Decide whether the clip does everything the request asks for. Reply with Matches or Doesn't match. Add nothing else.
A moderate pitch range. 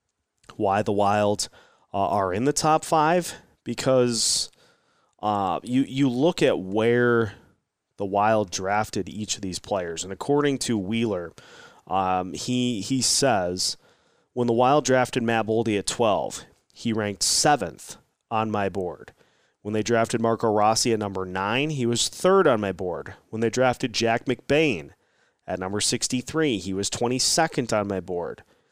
Matches